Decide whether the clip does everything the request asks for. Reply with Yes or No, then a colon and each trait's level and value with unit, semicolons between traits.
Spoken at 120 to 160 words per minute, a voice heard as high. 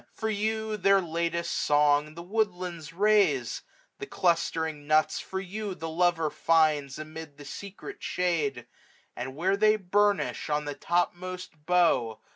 No: average, 140 wpm; medium, 170 Hz